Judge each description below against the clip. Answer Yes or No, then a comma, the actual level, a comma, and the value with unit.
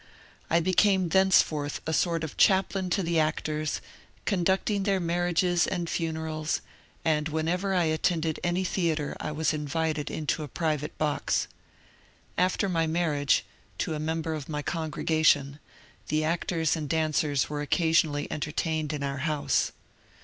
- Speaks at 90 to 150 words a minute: Yes, average, 140 wpm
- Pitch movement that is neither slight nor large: No, narrow, 2.3 semitones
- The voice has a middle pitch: Yes, medium, 160 Hz